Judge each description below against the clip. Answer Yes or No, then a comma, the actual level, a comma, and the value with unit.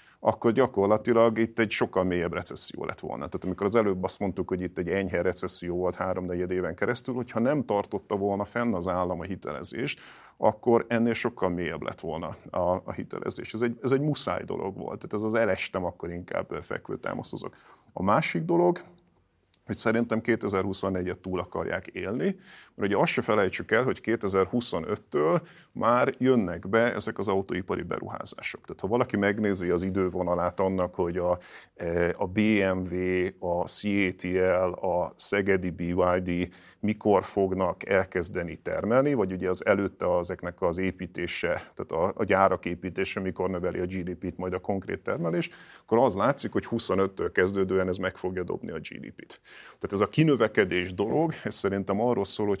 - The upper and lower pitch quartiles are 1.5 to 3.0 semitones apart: No, average, 3.5 semitones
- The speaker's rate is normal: No, fast, 160 wpm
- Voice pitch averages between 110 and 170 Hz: No, very low, 95 Hz